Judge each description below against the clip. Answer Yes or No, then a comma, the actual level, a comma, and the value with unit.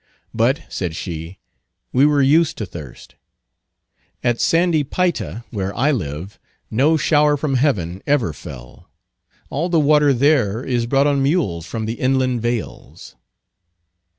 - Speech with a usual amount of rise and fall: No, wide, 6.9 semitones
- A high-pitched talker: No, low, 130 Hz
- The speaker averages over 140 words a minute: No, slow, 135 wpm